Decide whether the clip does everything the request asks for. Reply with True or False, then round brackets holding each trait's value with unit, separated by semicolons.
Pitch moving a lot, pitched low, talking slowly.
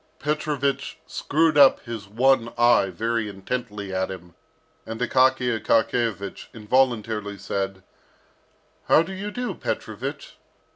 False (4.8 semitones; 115 Hz; 110 wpm)